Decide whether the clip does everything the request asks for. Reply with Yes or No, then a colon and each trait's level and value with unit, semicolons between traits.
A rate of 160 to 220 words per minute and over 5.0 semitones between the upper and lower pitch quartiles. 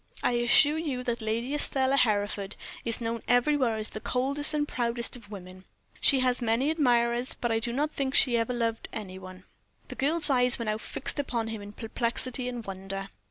No: average, 200 wpm; average, 3.1 semitones